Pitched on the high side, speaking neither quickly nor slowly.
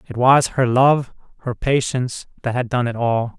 No: low, 125 Hz; average, 195 wpm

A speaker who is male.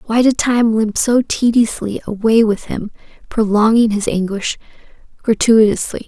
No: female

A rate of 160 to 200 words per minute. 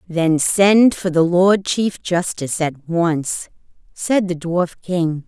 No: average, 150 wpm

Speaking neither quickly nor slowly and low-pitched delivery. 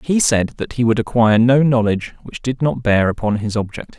No: fast, 225 wpm; low, 115 Hz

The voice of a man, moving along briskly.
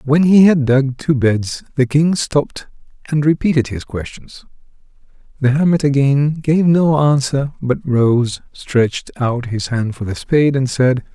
No: male; average, 160 wpm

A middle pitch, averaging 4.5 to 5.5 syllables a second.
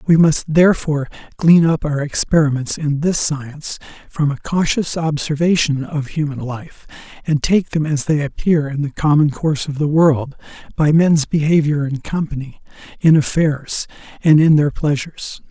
Yes: medium, 150 Hz; 4.8 syllables/s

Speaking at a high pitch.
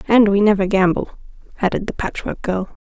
Yes: high, 200 Hz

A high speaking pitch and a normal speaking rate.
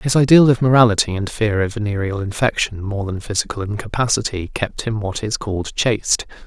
No: low, 110 Hz; average, 175 wpm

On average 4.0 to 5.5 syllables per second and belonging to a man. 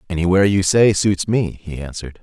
No: 5.9 syllables/s; male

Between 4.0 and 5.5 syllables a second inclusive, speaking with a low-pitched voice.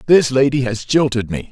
Yes: 5.3 syllables/s; low, 130 Hz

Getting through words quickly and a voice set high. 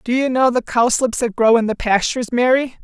Yes: fast, 235 wpm; high, 240 Hz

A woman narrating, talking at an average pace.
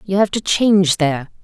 No: female; fast, 210 wpm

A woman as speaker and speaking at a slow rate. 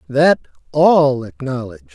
No: male; slow, 90 wpm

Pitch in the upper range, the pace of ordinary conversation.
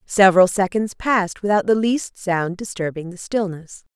Yes: high, 195 Hz; average, 150 wpm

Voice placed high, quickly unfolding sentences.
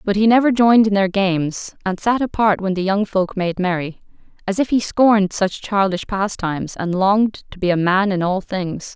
Yes: high, 195 Hz; fast, 215 wpm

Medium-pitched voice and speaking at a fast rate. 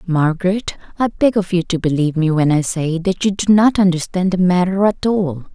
Yes: medium, 180 Hz; fast, 215 wpm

